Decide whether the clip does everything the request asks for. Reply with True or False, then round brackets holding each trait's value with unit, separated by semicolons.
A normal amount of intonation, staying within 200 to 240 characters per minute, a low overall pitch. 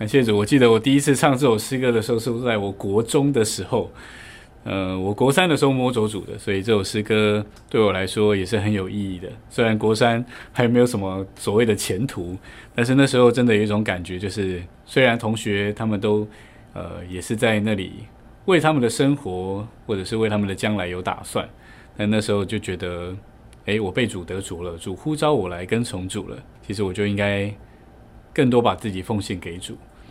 False (3.6 semitones; 300 characters per minute; 105 Hz)